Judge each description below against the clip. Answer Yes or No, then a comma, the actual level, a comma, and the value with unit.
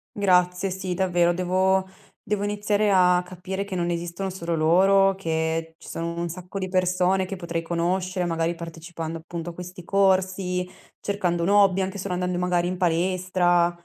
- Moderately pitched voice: Yes, medium, 180 Hz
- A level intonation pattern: Yes, narrow, 1.7 semitones